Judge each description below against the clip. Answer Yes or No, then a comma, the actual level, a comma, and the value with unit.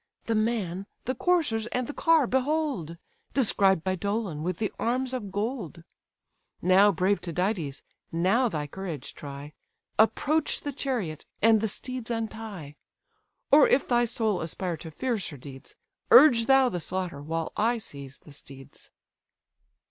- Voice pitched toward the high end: Yes, high, 205 Hz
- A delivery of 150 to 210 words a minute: No, average, 140 wpm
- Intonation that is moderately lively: No, wide, 6.6 semitones